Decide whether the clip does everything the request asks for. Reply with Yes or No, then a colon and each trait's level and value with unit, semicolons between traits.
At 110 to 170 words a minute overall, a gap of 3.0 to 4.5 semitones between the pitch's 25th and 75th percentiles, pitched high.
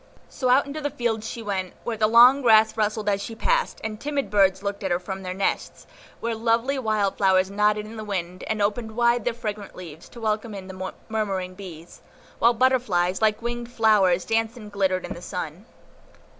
No: average, 200 wpm; average, 3.4 semitones; high, 215 Hz